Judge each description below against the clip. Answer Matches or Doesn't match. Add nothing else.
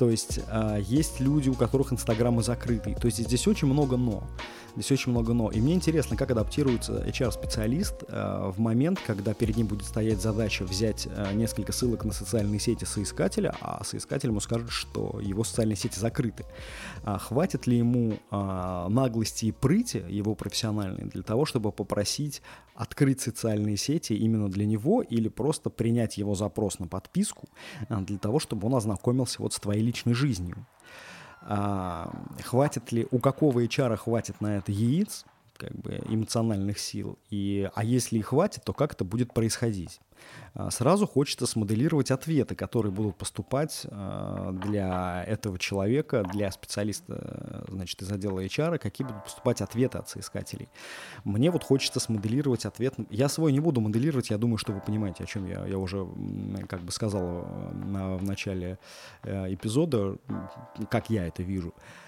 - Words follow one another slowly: Doesn't match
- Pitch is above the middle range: Doesn't match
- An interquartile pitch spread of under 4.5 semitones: Matches